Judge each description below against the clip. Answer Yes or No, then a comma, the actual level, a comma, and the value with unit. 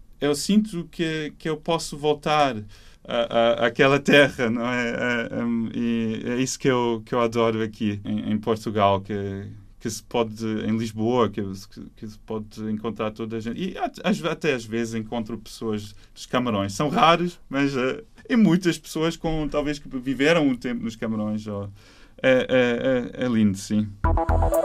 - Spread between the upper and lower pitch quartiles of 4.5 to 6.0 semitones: Yes, wide, 5.4 semitones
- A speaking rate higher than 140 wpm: Yes, average, 180 wpm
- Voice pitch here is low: Yes, low, 115 Hz